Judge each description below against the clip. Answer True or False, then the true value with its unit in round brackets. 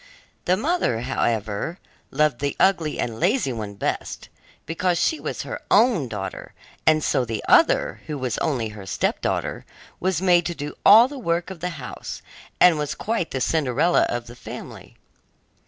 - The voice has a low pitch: False (155 Hz)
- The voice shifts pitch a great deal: True (6.9 semitones)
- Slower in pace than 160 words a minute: False (165 wpm)